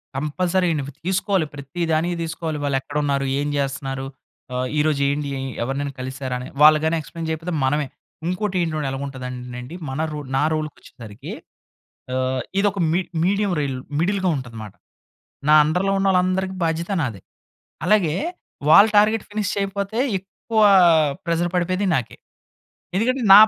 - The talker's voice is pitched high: No, medium, 160 Hz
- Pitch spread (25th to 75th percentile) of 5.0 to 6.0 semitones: Yes, wide, 5.5 semitones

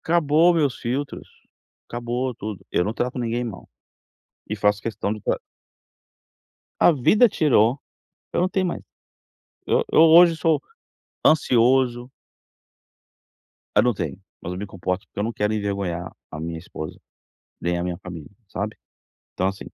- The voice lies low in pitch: Yes, low, 115 Hz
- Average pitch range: No, wide, 6.6 semitones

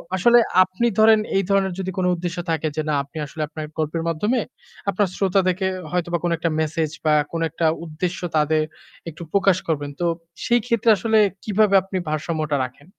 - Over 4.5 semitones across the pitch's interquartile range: No, average, 3.8 semitones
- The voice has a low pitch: No, medium, 175 Hz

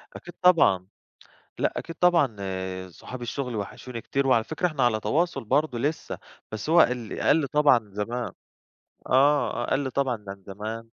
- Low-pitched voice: Yes, low, 125 Hz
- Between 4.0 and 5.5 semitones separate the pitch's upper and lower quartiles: Yes, average, 5.1 semitones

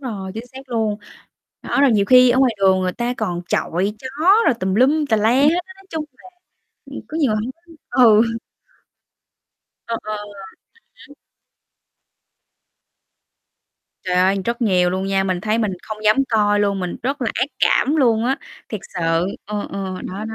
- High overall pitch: Yes, high, 220 Hz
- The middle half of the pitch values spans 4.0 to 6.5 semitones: Yes, average, 4.7 semitones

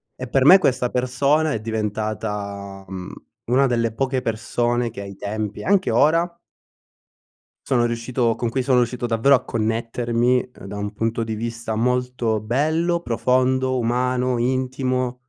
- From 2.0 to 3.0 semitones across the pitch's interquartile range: Yes, narrow, 2.4 semitones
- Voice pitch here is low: Yes, low, 120 Hz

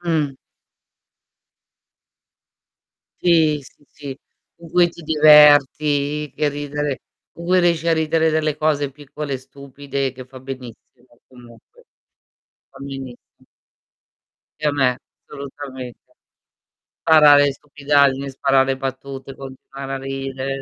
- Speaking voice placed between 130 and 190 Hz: Yes, medium, 140 Hz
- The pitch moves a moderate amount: No, narrow, 2.1 semitones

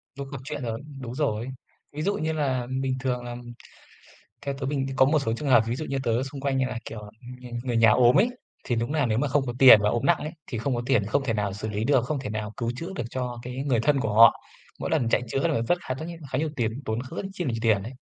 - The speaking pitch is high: No, low, 130 Hz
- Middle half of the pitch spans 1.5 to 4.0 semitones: Yes, average, 3.5 semitones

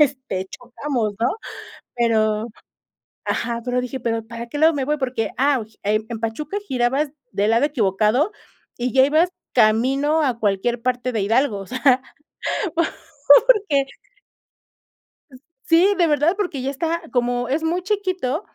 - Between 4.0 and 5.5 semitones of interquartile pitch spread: Yes, average, 4.5 semitones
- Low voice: No, very high, 255 Hz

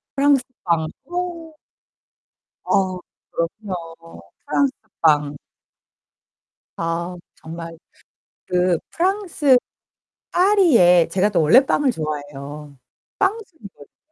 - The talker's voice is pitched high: No, medium, 180 Hz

